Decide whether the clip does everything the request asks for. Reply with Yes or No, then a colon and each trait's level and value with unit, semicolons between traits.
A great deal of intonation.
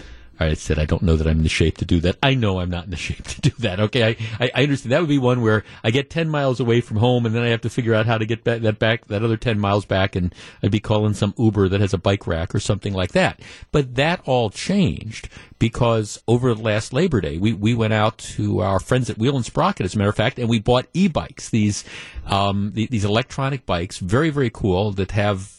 No: average, 3.5 semitones